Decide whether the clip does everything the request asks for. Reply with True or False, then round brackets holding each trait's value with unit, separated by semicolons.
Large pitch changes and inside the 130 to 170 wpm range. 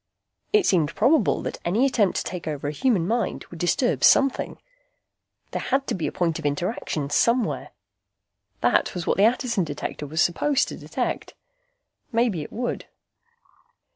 True (7.1 semitones; 160 wpm)